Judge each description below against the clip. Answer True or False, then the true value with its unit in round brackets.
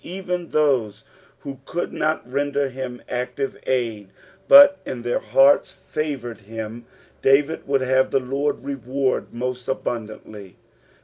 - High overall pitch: False (130 Hz)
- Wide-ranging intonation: False (2.9 semitones)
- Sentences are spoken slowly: True (125 wpm)